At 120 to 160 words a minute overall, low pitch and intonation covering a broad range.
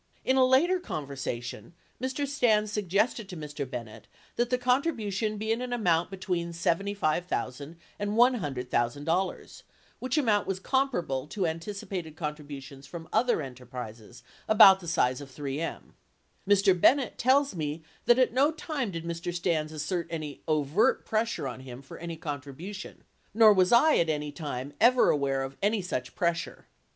No: average, 150 wpm; medium, 175 Hz; wide, 7.3 semitones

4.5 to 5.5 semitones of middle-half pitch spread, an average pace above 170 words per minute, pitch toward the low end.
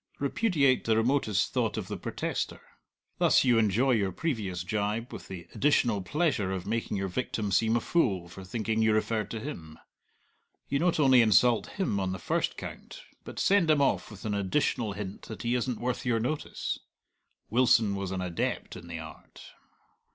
Yes: average, 4.8 semitones; average, 180 wpm; low, 110 Hz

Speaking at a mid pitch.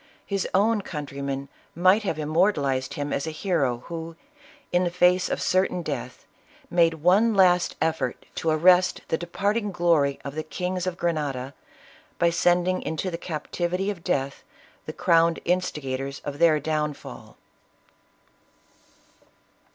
Yes: medium, 170 Hz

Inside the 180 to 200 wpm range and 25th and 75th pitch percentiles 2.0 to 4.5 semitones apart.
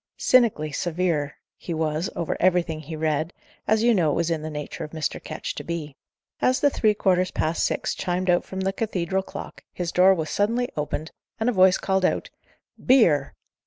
Yes: average, 195 wpm; average, 3.6 semitones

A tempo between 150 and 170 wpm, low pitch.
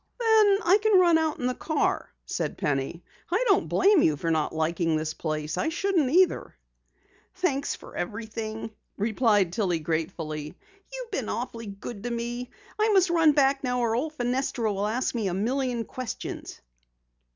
No: average, 165 wpm; high, 240 Hz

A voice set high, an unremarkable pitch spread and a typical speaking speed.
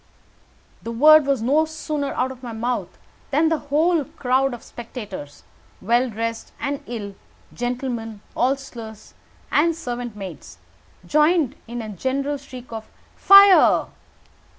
No: very high, 250 Hz; average, 4.1 semitones; slow, 130 wpm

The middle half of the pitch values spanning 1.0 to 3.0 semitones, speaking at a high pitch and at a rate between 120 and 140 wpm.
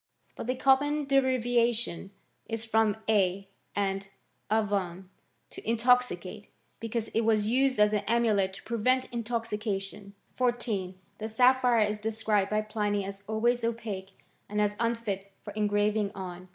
Yes: average, 2.7 semitones; high, 215 Hz; slow, 135 wpm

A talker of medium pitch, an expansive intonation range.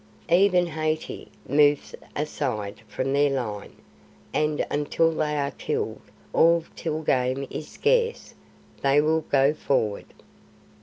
No: medium, 150 Hz; narrow, 2.6 semitones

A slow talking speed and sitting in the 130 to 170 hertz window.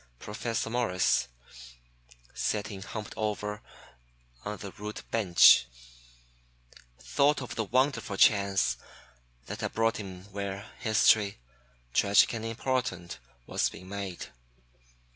No: slow, 105 wpm; low, 105 Hz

